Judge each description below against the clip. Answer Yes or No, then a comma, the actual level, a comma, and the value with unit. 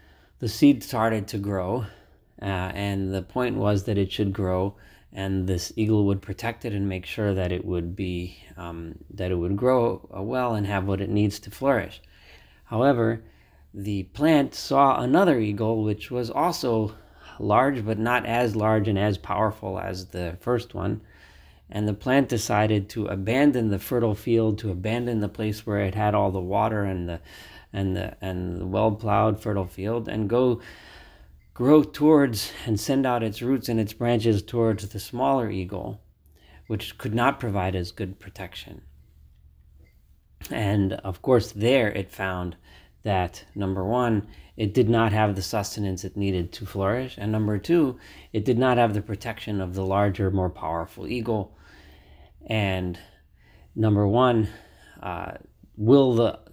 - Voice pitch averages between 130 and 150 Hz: No, low, 105 Hz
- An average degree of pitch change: Yes, average, 3.4 semitones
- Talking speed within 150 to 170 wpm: Yes, average, 160 wpm